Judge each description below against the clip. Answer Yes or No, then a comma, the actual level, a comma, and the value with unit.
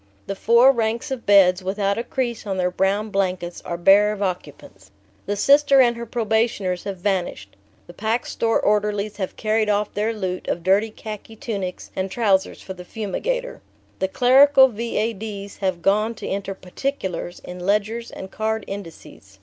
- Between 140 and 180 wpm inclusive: Yes, average, 165 wpm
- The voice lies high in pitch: Yes, high, 205 Hz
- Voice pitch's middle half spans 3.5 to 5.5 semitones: No, average, 3.0 semitones